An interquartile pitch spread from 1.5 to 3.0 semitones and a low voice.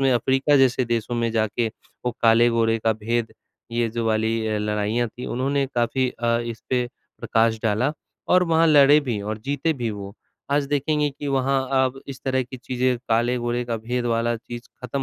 Yes: average, 2.7 semitones; low, 120 Hz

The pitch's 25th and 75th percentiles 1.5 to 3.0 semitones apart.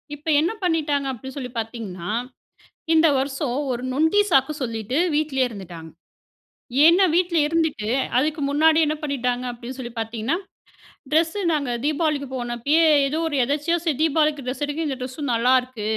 No: average, 4.2 semitones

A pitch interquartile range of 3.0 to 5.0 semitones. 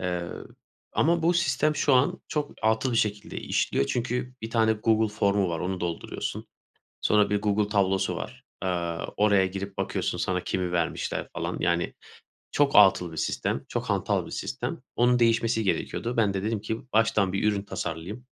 Yes: average, 3.5 semitones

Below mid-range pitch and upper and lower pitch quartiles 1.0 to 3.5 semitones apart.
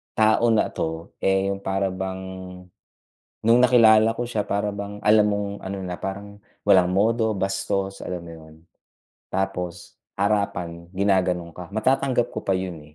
Yes: low, 100 Hz; narrow, 2.6 semitones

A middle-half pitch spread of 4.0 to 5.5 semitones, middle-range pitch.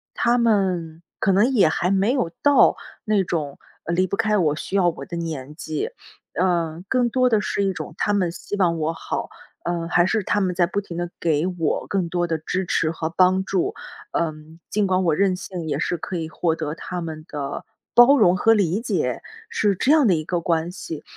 No: average, 3.5 semitones; medium, 175 Hz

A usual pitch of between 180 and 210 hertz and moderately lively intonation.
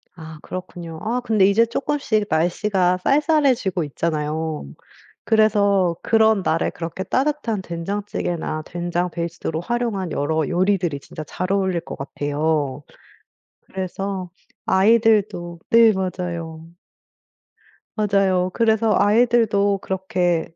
Yes: high, 190 Hz; average, 4.2 semitones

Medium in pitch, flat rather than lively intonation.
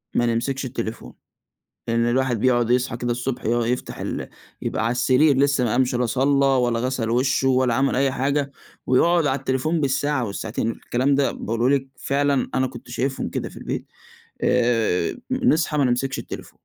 No: low, 130 Hz; narrow, 2.3 semitones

